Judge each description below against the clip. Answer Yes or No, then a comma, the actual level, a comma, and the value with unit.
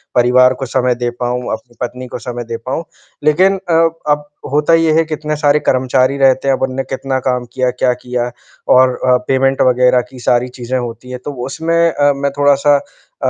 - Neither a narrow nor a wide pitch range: No, narrow, 2.3 semitones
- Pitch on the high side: No, low, 130 Hz